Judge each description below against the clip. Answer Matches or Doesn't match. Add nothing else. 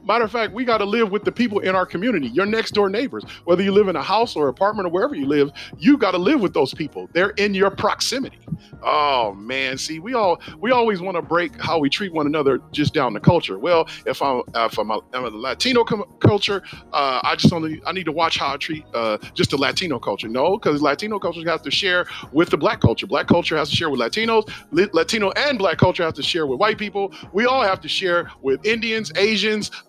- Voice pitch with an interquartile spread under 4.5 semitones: Doesn't match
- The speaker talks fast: Matches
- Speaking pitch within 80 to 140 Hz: Doesn't match